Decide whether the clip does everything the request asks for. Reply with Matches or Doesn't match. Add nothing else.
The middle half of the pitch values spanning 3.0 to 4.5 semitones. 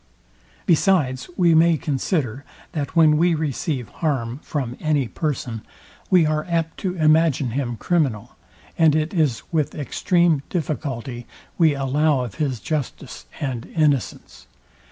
Matches